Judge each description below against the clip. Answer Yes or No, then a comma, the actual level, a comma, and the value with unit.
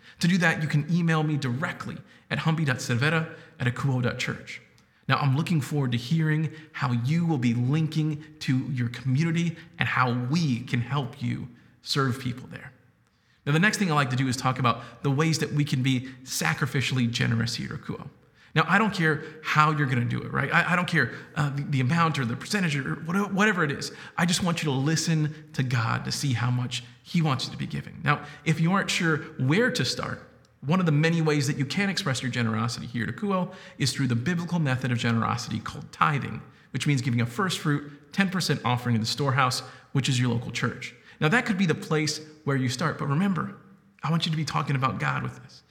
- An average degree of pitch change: Yes, average, 4.1 semitones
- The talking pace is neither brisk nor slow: No, fast, 225 wpm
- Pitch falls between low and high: Yes, medium, 145 Hz